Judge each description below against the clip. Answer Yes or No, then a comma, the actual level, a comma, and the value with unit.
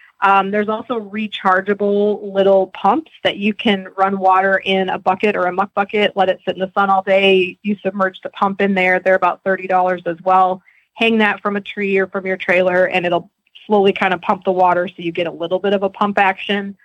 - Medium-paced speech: No, fast, 230 wpm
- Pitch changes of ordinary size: No, narrow, 1.5 semitones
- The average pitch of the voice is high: Yes, high, 195 Hz